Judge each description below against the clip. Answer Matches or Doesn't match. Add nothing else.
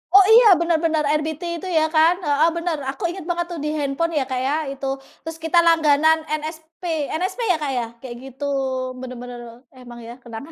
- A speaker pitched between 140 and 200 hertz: Doesn't match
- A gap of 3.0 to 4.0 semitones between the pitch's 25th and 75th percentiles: Matches